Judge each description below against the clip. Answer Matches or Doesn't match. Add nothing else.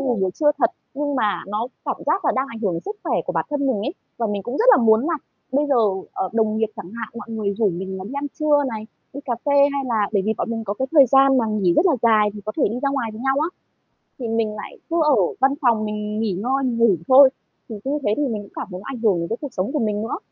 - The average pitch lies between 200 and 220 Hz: Doesn't match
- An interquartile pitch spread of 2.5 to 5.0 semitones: Matches